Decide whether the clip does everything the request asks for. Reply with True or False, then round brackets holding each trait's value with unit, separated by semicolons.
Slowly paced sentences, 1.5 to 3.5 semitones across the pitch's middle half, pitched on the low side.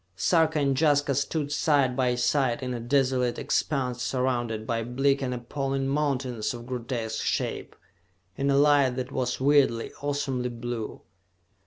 False (145 wpm; 2.5 semitones; 130 Hz)